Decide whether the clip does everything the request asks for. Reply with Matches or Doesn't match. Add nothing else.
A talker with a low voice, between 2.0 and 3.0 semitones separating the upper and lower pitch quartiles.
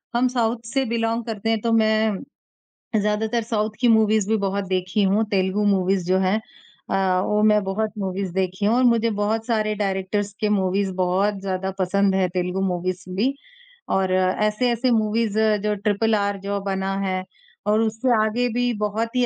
Doesn't match